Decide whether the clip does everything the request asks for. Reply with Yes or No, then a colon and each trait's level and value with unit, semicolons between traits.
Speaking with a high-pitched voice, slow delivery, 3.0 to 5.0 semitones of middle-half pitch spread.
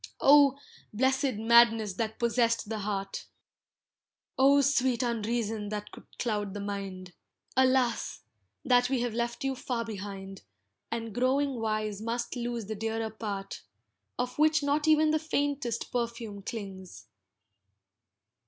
Yes: high, 235 Hz; slow, 125 wpm; average, 3.6 semitones